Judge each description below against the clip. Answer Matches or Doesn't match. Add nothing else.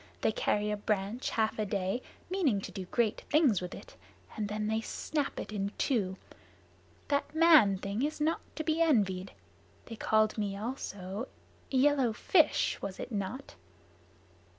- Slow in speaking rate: Doesn't match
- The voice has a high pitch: Matches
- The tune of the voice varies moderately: Doesn't match